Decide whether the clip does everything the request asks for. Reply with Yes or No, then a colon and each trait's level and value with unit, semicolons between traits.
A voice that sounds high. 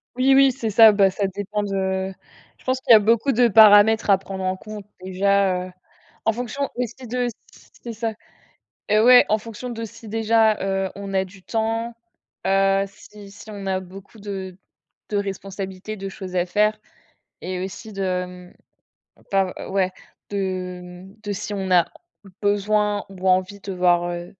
Yes: high, 200 Hz